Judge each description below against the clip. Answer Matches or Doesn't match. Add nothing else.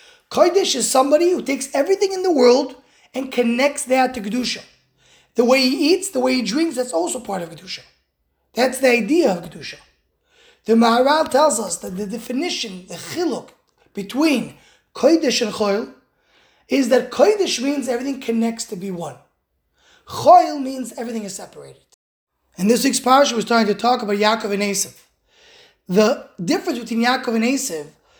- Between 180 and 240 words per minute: Doesn't match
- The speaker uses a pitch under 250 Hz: Doesn't match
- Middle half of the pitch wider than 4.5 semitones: Matches